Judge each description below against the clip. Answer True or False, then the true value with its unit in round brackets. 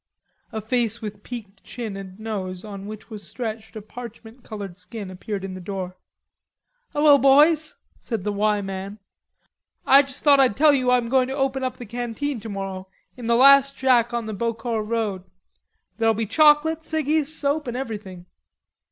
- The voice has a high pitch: True (230 Hz)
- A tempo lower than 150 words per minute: False (170 wpm)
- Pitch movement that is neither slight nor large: True (4.7 semitones)